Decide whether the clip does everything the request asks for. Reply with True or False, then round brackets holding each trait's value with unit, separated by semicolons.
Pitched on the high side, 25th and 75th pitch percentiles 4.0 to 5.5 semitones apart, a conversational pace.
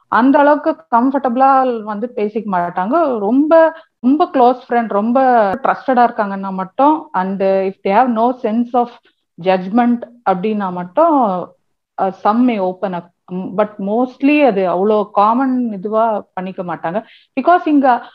True (230 Hz; 5.2 semitones; 120 wpm)